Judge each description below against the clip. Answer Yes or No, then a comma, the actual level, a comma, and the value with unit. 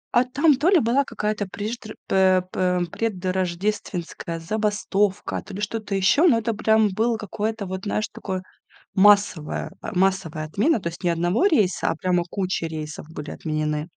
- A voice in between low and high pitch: No, high, 195 Hz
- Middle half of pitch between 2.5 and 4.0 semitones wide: Yes, average, 3.5 semitones